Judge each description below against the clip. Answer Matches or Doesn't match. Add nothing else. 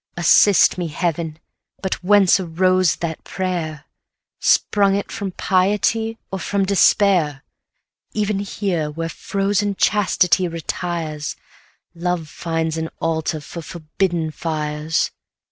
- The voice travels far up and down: Doesn't match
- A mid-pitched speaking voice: Matches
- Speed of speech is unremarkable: Doesn't match